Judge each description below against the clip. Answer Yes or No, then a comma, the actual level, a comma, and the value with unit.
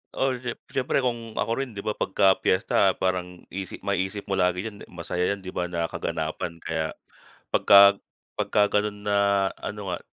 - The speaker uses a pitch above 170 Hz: No, low, 100 Hz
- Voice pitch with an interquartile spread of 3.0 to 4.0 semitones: No, narrow, 2.4 semitones